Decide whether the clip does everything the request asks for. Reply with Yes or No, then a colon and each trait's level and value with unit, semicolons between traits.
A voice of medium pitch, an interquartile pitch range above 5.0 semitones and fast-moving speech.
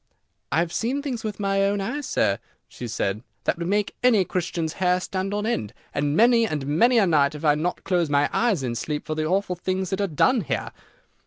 Yes: medium, 180 Hz; wide, 5.4 semitones; fast, 225 wpm